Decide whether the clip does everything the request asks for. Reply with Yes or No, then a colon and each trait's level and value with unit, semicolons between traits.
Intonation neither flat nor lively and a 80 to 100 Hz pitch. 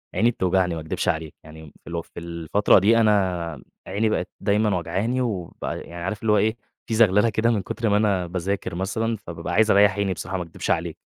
Yes: average, 4.1 semitones; very low, 95 Hz